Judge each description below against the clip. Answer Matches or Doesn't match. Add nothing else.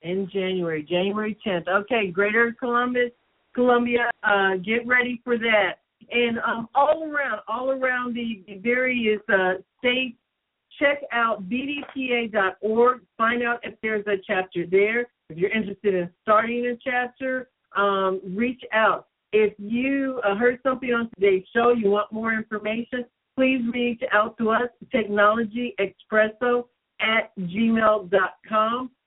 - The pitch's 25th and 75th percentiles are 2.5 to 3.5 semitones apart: Matches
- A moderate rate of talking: Doesn't match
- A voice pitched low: Doesn't match